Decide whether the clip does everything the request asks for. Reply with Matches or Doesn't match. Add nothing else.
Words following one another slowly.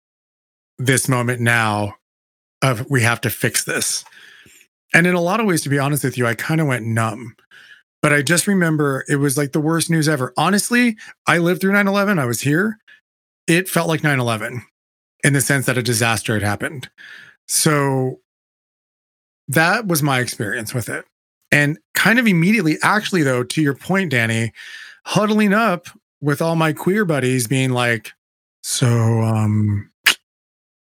Doesn't match